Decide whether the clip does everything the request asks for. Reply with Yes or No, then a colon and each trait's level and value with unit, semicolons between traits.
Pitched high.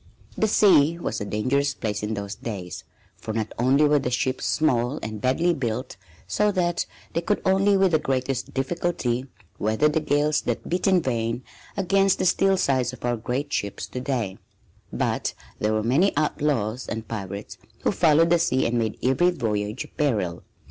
No: low, 130 Hz